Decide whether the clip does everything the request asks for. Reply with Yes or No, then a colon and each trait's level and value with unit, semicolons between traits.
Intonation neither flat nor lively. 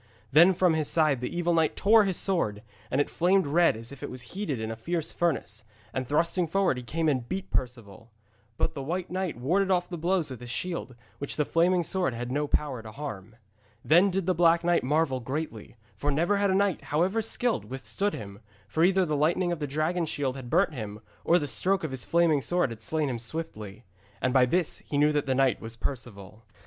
No: wide, 5.7 semitones